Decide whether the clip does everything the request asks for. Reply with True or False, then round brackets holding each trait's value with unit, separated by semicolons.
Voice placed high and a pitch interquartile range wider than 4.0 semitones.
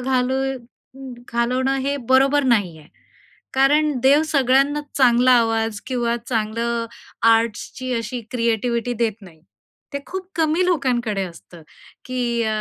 False (245 Hz; 3.0 semitones)